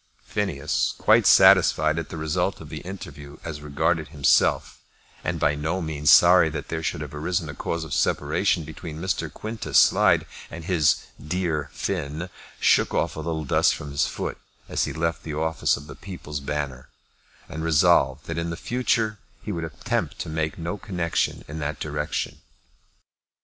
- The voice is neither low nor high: No, very low, 80 Hz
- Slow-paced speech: No, average, 170 wpm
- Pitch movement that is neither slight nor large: No, narrow, 2.1 semitones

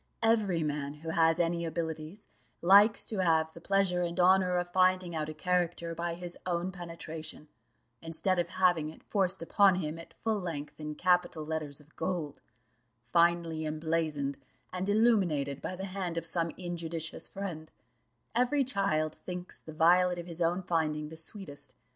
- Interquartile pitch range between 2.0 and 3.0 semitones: Yes, narrow, 2.6 semitones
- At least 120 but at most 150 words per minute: No, average, 160 wpm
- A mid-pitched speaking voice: Yes, medium, 170 Hz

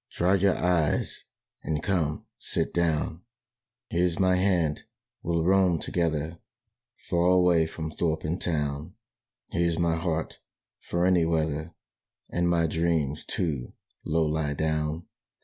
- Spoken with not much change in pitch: Yes, narrow, 2.0 semitones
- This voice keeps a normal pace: No, slow, 125 wpm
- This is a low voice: Yes, very low, 85 Hz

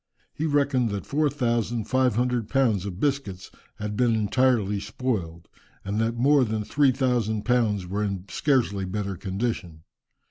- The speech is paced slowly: No, average, 150 wpm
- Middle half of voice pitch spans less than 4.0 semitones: No, average, 4.3 semitones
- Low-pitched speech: Yes, low, 115 Hz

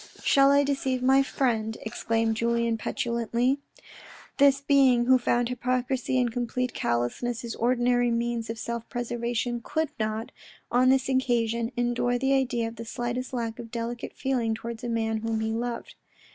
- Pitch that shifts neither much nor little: No, narrow, 1.8 semitones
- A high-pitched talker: Yes, high, 240 Hz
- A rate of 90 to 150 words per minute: No, average, 160 wpm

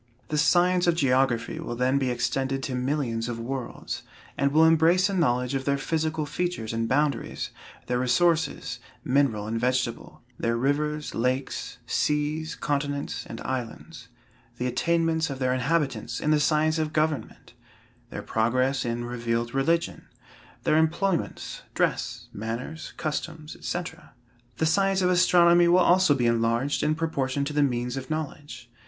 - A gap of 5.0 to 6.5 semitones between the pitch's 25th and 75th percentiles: No, average, 4.3 semitones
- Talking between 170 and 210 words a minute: No, average, 150 wpm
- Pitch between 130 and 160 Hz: Yes, medium, 140 Hz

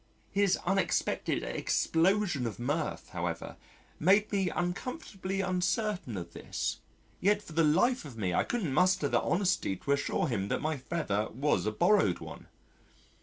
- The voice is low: No, medium, 175 Hz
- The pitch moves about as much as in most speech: No, wide, 6.8 semitones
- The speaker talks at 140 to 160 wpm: Yes, average, 150 wpm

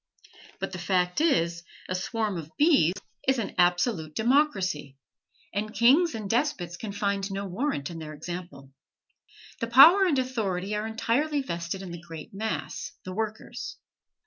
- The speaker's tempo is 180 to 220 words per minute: No, average, 150 wpm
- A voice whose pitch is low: No, high, 200 Hz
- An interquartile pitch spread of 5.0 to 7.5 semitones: Yes, average, 5.3 semitones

